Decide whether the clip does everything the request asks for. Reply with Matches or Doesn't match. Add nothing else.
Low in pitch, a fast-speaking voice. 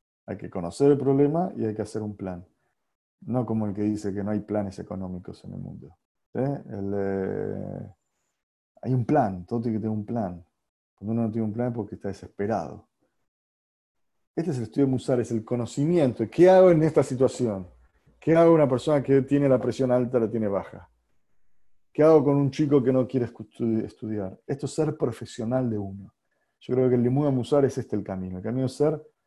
Matches